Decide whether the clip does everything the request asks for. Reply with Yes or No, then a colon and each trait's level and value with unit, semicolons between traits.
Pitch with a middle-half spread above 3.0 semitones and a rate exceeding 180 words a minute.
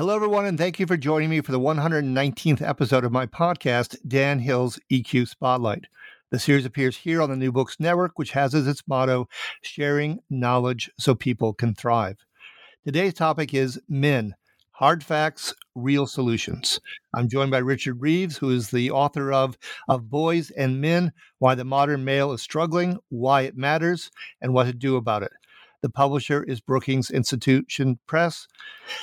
No: average, 3.4 semitones; average, 170 wpm